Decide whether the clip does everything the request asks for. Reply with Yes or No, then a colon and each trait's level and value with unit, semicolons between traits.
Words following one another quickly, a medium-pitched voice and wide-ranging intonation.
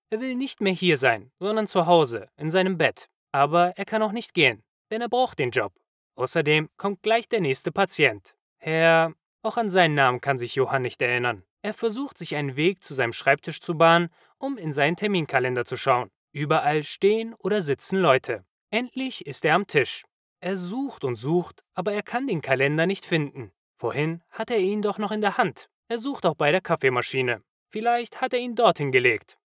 Yes: fast, 200 wpm; medium, 175 Hz; wide, 7.1 semitones